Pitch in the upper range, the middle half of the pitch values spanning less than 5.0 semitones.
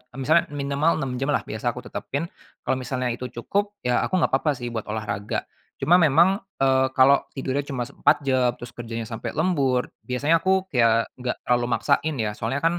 No: low, 135 Hz; average, 4.0 semitones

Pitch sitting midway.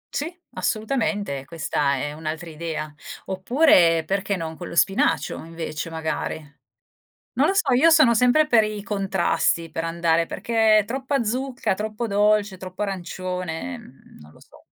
No: high, 195 Hz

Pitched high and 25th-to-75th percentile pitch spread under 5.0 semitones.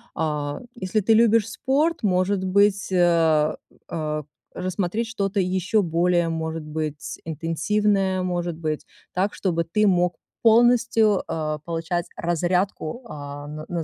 No: medium, 180 Hz; average, 4.1 semitones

